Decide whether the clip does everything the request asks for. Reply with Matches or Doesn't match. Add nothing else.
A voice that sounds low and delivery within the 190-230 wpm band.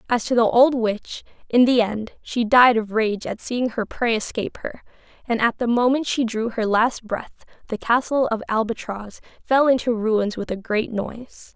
Doesn't match